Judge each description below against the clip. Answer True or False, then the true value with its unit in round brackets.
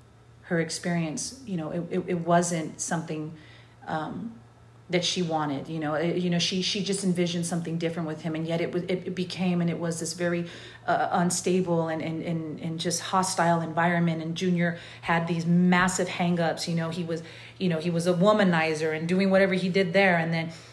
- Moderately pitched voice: True (170 Hz)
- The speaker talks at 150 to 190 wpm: False (205 wpm)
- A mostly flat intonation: True (1.8 semitones)